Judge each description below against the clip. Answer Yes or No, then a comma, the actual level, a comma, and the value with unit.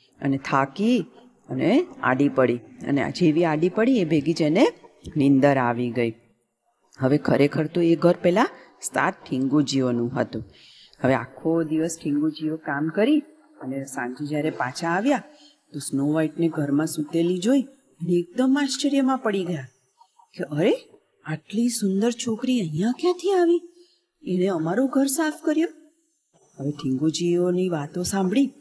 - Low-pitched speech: No, medium, 175 Hz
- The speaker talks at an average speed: Yes, average, 120 wpm